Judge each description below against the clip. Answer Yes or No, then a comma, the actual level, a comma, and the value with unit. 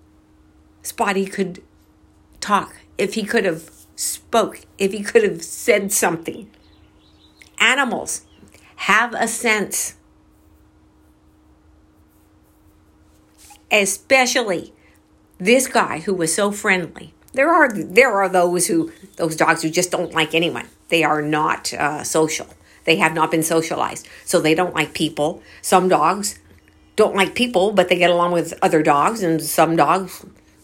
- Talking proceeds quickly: No, slow, 135 wpm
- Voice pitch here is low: No, medium, 160 Hz